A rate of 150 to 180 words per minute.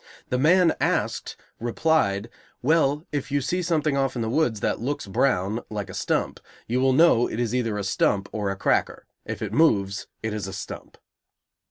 No: average, 190 wpm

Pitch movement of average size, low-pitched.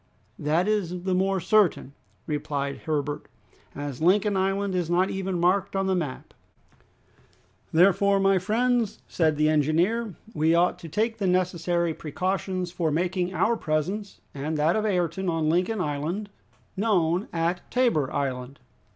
No: average, 3.7 semitones; medium, 180 Hz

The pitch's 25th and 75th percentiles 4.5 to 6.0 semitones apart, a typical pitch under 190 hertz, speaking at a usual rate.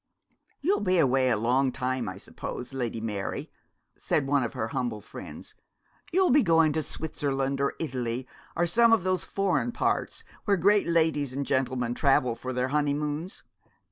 Yes: average, 5.0 semitones; medium, 140 Hz; average, 165 wpm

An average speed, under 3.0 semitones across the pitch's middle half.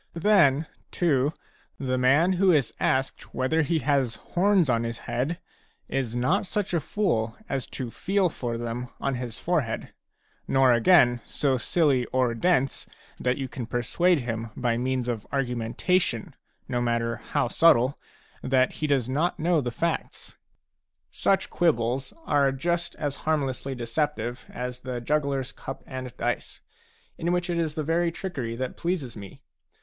No: average, 155 wpm; average, 5.1 semitones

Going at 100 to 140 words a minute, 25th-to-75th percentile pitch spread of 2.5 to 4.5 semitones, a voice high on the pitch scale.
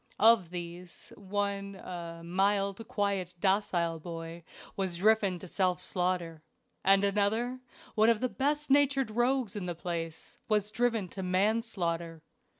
Yes: slow, 135 wpm; average, 3.8 semitones; high, 195 Hz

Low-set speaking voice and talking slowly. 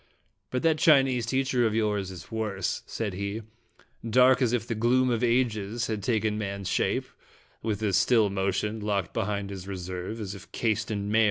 No: low, 110 Hz; average, 180 wpm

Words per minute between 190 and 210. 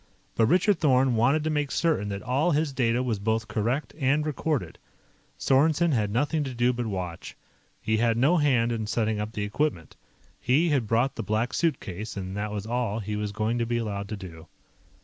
Yes: average, 200 wpm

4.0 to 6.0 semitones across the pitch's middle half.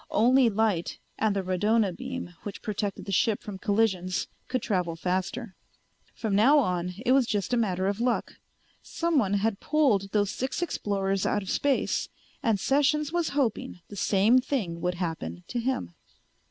Yes: average, 5.1 semitones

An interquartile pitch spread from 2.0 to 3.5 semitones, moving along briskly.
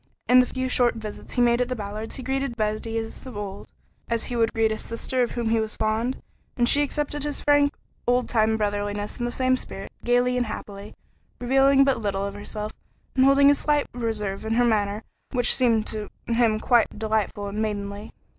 Yes: average, 2.9 semitones; fast, 210 wpm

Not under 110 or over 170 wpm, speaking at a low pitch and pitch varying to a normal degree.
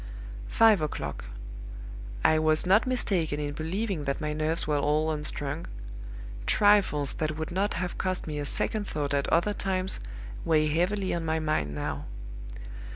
No: average, 155 wpm; medium, 160 Hz; average, 3.9 semitones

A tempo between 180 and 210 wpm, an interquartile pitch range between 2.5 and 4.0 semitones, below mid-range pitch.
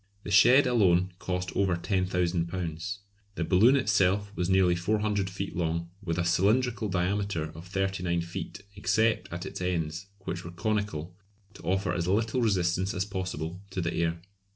No: average, 155 wpm; average, 2.8 semitones; very low, 95 Hz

